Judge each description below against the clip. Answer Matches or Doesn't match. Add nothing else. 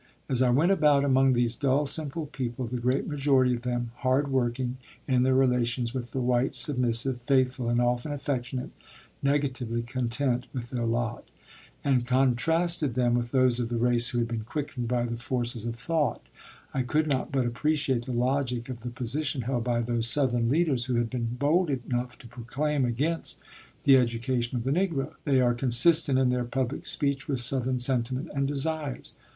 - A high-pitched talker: Doesn't match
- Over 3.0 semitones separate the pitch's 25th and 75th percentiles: Doesn't match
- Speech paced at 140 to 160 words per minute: Doesn't match